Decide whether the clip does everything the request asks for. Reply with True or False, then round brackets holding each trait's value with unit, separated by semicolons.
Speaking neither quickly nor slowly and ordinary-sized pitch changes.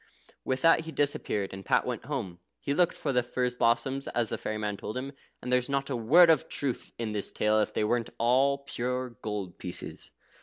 False (215 wpm; 4.2 semitones)